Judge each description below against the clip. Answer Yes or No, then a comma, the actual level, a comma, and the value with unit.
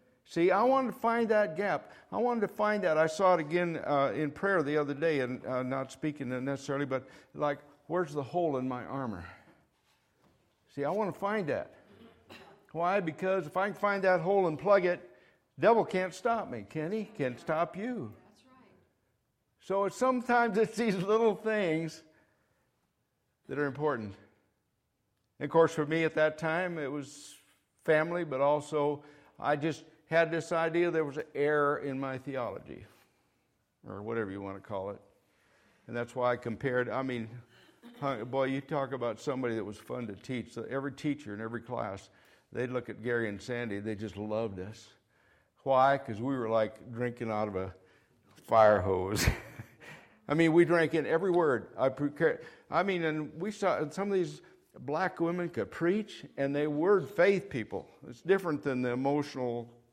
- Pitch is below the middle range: No, medium, 145 Hz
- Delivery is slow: No, average, 180 wpm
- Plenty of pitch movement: Yes, wide, 6.1 semitones